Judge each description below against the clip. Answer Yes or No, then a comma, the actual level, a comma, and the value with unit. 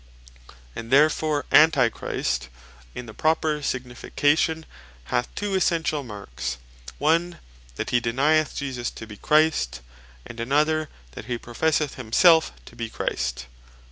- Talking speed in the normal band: No, slow, 120 wpm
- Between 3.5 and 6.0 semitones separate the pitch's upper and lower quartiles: Yes, average, 5.2 semitones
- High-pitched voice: No, medium, 140 Hz